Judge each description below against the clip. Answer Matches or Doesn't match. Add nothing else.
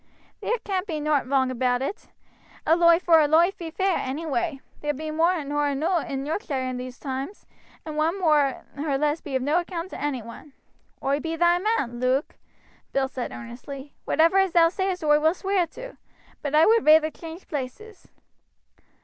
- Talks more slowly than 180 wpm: Doesn't match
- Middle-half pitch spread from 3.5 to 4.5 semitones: Matches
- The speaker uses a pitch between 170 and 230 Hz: Doesn't match